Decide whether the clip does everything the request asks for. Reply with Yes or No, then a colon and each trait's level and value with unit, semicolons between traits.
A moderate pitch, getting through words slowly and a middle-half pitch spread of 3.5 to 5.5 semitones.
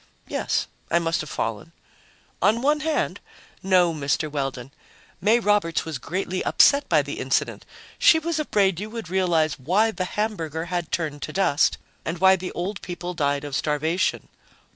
No: medium, 175 Hz; average, 165 wpm; average, 4.7 semitones